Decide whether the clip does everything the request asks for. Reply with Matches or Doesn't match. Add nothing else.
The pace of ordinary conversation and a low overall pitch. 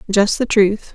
Doesn't match